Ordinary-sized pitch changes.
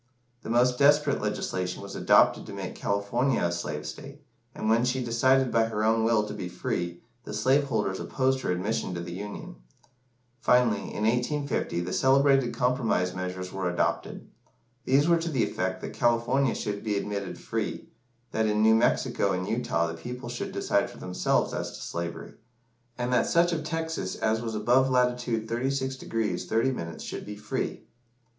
Yes: average, 4.6 semitones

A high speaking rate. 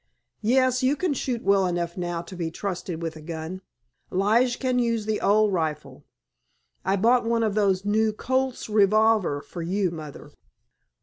No: average, 165 wpm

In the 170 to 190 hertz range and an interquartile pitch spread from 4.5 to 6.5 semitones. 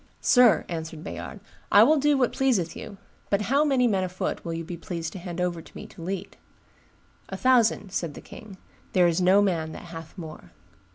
Yes: medium, 185 Hz; average, 5.2 semitones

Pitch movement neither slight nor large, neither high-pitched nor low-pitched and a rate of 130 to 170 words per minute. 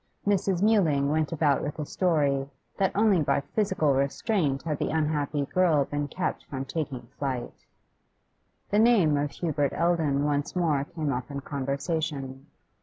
Yes: average, 3.7 semitones; medium, 150 Hz; average, 150 wpm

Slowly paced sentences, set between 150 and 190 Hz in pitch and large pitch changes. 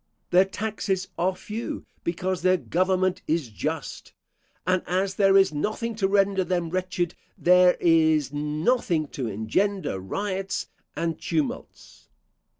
No: slow, 125 wpm; medium, 185 Hz; average, 3.1 semitones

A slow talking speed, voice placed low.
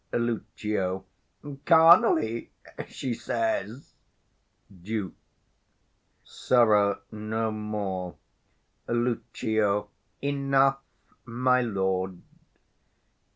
Yes: slow, 55 wpm; low, 110 Hz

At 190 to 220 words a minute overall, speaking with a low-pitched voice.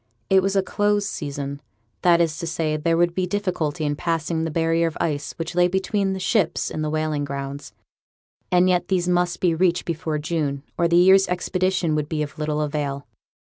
No: average, 200 wpm; medium, 165 Hz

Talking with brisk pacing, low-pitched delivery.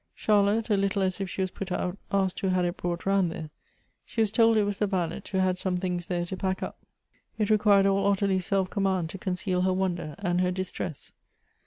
No: fast, 225 wpm; high, 190 Hz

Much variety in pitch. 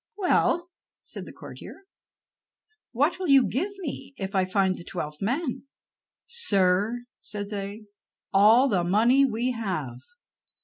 Yes: wide, 6.1 semitones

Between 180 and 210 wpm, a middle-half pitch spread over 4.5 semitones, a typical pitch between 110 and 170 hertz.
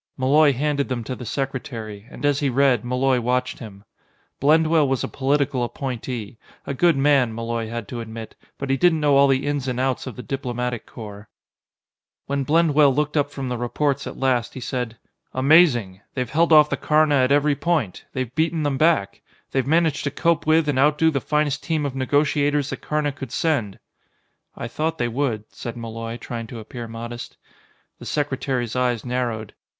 No: average, 185 wpm; average, 3.5 semitones; low, 135 Hz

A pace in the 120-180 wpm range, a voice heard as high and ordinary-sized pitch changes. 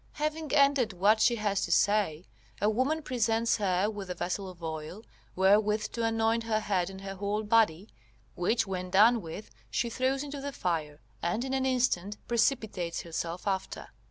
Yes: average, 175 wpm; high, 210 Hz; average, 4.2 semitones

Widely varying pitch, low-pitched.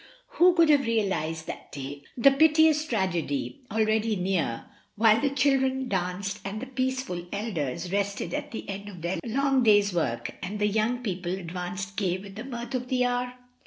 No: wide, 5.8 semitones; high, 210 Hz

